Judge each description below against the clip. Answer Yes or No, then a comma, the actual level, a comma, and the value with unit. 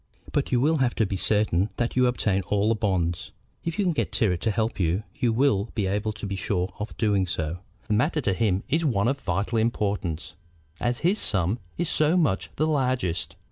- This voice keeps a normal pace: No, fast, 215 wpm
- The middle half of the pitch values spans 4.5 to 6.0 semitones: Yes, average, 4.8 semitones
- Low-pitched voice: Yes, low, 110 Hz